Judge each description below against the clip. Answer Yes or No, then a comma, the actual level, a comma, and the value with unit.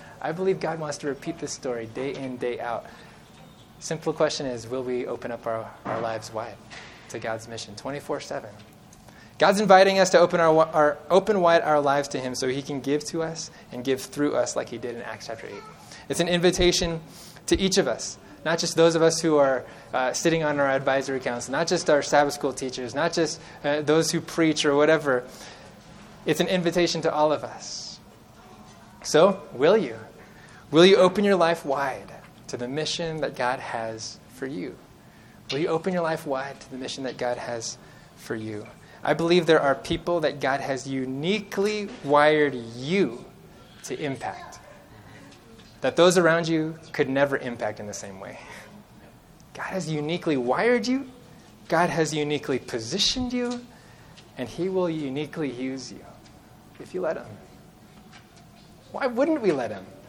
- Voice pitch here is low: No, medium, 150 Hz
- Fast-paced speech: No, average, 180 wpm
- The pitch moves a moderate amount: Yes, average, 4.5 semitones